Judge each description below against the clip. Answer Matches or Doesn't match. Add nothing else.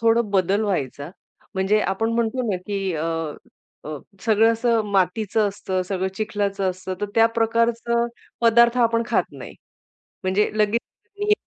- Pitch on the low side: Doesn't match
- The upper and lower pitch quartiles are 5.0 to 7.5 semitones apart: Doesn't match